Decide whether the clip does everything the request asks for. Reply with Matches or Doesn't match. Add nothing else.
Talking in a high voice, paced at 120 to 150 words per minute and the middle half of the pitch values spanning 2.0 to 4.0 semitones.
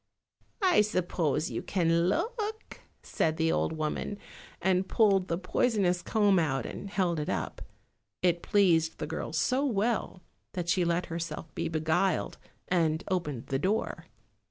Doesn't match